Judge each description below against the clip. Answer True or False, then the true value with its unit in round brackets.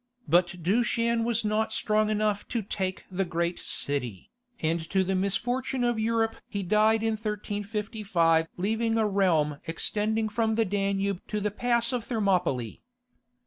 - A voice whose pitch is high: True (210 Hz)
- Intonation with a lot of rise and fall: False (3.3 semitones)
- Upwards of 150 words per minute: False (145 wpm)